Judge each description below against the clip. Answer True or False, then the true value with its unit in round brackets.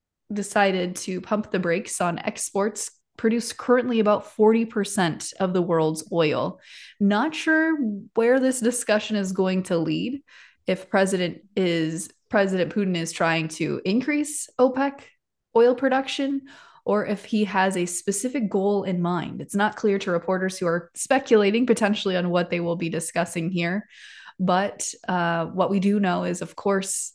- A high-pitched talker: True (200 Hz)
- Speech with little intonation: False (4.1 semitones)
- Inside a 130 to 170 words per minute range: True (155 wpm)